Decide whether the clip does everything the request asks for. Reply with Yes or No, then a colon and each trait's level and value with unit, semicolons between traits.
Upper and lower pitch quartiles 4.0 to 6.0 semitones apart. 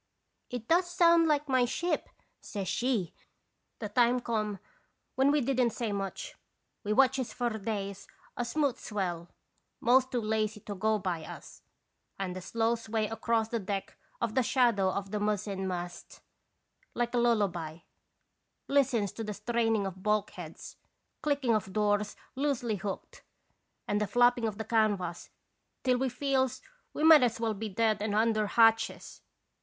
No: average, 3.4 semitones